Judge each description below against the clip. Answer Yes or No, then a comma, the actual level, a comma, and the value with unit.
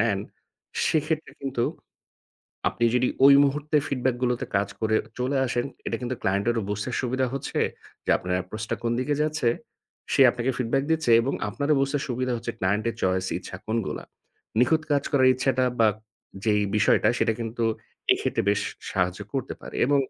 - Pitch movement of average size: Yes, average, 3.7 semitones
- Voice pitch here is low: Yes, low, 120 Hz